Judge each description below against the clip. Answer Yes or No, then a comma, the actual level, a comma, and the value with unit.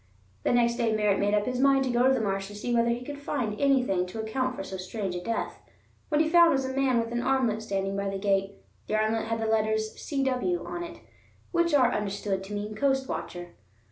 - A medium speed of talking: No, fast, 235 wpm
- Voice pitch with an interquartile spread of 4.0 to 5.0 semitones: Yes, average, 4.4 semitones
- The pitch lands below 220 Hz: No, high, 230 Hz